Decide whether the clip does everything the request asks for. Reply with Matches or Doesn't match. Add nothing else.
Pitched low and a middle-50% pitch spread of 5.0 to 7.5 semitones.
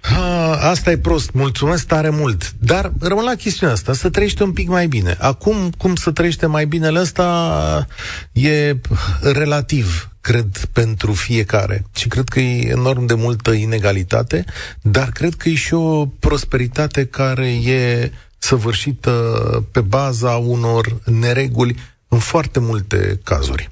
Matches